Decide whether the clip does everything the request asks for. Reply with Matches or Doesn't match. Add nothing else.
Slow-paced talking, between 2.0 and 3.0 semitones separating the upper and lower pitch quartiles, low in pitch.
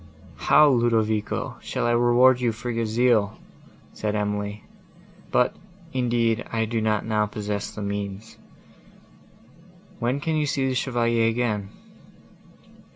Matches